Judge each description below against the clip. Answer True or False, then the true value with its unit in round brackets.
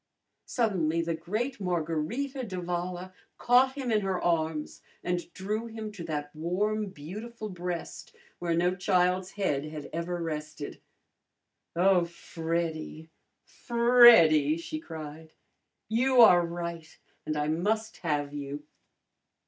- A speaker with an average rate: False (115 wpm)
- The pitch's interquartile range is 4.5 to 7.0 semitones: True (5.0 semitones)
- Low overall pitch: False (175 Hz)